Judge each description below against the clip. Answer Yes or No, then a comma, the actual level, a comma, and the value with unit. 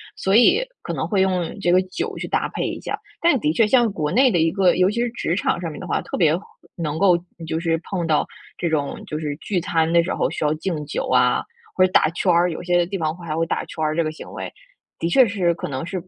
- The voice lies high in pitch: No, medium, 175 Hz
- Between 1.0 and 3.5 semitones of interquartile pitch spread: Yes, average, 3.1 semitones